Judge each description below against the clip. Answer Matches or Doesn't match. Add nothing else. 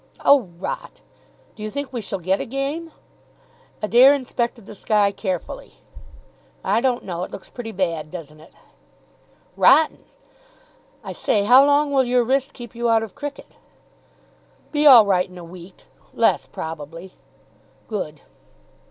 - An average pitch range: Doesn't match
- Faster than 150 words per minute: Doesn't match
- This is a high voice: Matches